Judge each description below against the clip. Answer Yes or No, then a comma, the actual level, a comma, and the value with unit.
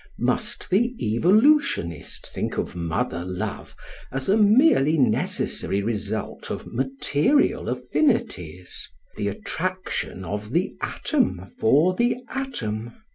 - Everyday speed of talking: No, slow, 115 wpm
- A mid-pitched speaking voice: No, low, 130 Hz